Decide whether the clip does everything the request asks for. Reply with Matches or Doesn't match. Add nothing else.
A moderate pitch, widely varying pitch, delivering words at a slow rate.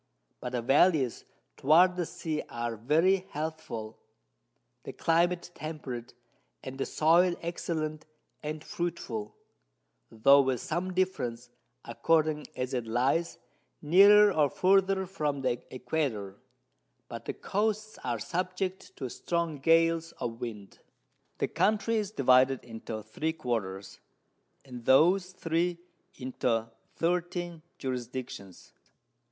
Matches